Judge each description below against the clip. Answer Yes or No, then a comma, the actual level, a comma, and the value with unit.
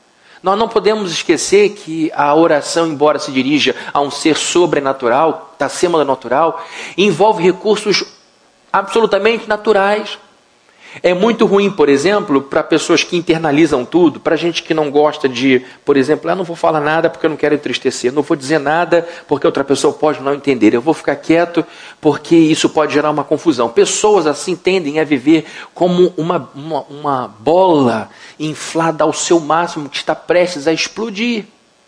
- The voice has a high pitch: No, medium, 165 Hz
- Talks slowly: No, average, 165 wpm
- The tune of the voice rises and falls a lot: No, average, 4.4 semitones